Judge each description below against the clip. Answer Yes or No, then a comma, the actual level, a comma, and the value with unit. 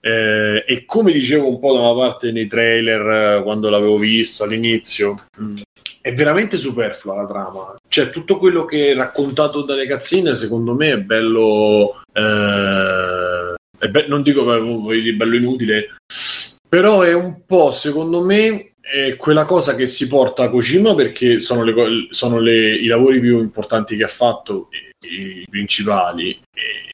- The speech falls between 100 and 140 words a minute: No, average, 165 wpm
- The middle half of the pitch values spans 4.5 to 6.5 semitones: Yes, wide, 5.4 semitones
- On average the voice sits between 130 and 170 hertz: No, low, 120 Hz